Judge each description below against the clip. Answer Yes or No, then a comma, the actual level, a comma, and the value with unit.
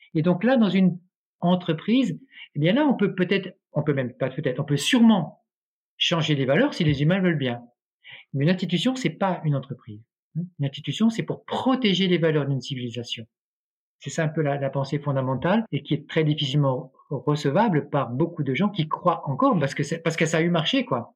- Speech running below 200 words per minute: No, average, 215 wpm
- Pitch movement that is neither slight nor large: Yes, average, 4.7 semitones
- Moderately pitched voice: Yes, medium, 160 Hz